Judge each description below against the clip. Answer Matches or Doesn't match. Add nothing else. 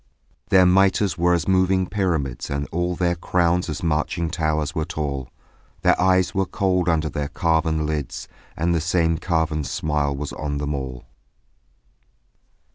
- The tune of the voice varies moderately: Matches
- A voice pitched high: Doesn't match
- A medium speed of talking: Matches